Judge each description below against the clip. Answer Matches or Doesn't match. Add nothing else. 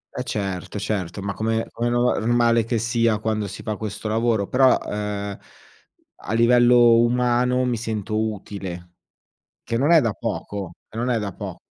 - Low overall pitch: Matches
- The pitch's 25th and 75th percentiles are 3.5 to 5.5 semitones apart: Doesn't match